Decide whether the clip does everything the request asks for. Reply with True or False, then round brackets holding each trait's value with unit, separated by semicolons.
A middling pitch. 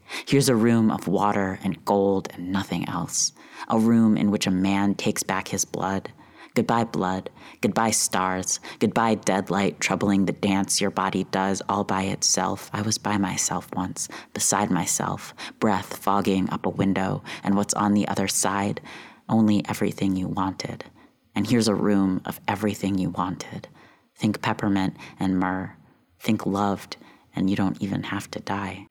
False (100 Hz)